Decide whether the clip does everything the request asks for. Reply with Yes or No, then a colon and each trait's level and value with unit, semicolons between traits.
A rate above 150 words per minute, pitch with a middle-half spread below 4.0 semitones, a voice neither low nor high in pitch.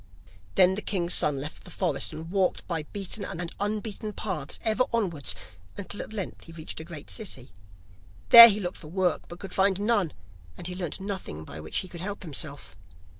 No: average, 195 wpm; average, 4.3 semitones; medium, 180 Hz